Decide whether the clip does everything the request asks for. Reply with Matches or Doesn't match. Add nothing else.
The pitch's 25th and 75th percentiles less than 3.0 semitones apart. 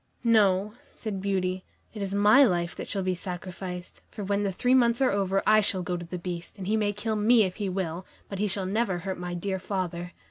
Matches